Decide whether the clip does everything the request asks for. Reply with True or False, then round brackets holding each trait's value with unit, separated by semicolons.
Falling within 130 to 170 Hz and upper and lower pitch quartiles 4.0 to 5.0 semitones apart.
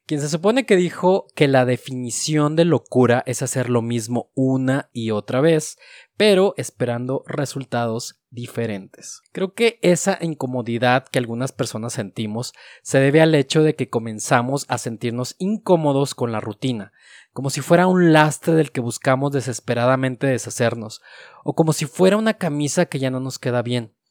True (135 Hz; 4.6 semitones)